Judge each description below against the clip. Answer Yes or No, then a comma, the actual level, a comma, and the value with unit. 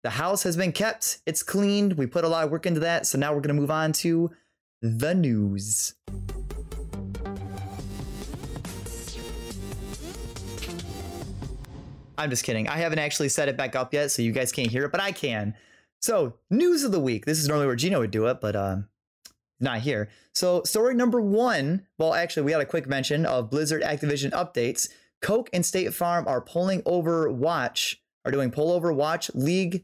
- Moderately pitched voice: Yes, medium, 145 Hz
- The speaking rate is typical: Yes, average, 185 wpm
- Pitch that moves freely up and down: Yes, wide, 7.5 semitones